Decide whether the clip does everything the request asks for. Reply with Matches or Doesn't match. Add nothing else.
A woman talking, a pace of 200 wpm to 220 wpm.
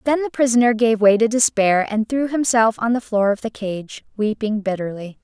Matches